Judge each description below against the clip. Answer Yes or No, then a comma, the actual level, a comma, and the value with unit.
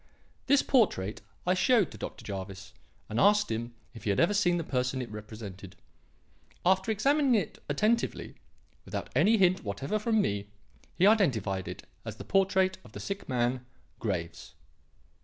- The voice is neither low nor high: Yes, medium, 145 Hz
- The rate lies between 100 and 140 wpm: No, average, 160 wpm